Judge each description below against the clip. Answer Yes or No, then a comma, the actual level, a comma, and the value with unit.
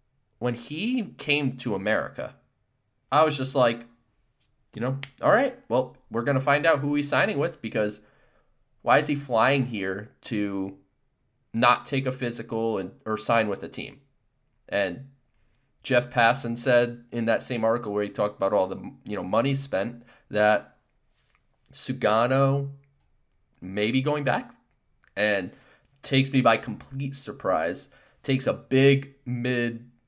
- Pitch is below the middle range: Yes, low, 125 Hz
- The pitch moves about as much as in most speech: Yes, average, 3.1 semitones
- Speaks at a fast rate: No, average, 145 wpm